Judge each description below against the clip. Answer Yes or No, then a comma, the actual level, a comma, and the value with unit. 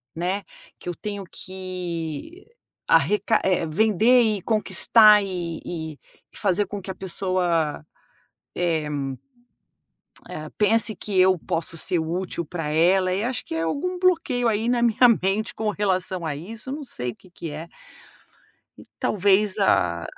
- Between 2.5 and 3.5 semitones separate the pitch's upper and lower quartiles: No, average, 4.2 semitones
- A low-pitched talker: No, high, 190 Hz